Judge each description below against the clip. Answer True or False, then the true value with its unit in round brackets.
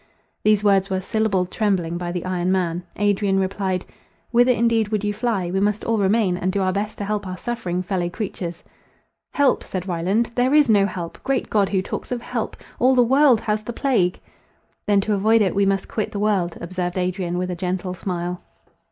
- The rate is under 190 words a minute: False (200 wpm)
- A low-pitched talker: False (195 Hz)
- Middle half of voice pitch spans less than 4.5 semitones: True (3.1 semitones)